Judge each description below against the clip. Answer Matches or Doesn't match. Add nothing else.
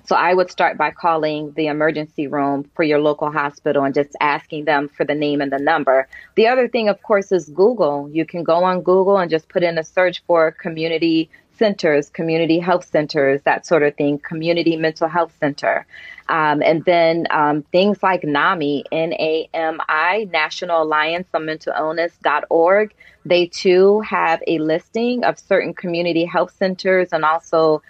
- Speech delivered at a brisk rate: Doesn't match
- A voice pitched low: Doesn't match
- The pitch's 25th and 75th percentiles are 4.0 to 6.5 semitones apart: Doesn't match